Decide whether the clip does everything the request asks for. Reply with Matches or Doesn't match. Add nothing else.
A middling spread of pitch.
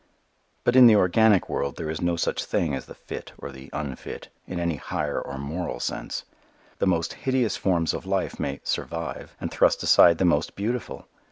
Matches